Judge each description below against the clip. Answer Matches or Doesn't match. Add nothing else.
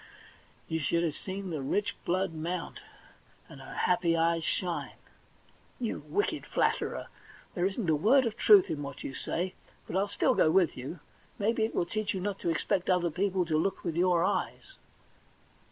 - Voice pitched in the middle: Matches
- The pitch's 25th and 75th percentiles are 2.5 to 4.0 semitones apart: Matches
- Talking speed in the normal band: Matches